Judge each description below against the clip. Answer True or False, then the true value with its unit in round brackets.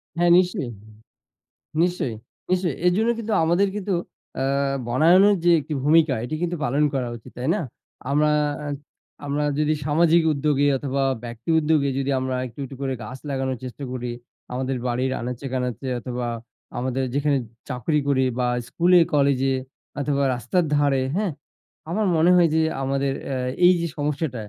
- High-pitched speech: False (140 Hz)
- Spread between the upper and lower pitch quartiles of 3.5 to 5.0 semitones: True (4.2 semitones)